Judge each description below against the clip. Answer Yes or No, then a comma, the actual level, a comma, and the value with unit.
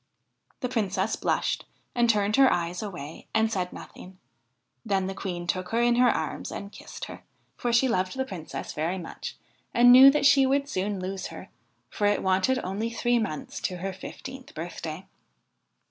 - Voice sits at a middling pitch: No, high, 200 Hz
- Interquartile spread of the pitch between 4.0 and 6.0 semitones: Yes, average, 4.7 semitones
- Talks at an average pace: Yes, average, 180 wpm